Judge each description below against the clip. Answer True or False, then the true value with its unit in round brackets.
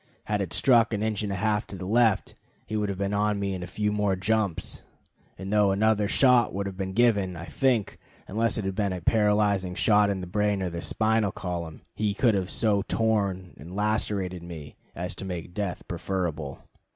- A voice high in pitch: False (100 Hz)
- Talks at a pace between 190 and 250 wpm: True (205 wpm)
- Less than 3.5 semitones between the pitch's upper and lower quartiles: True (2.6 semitones)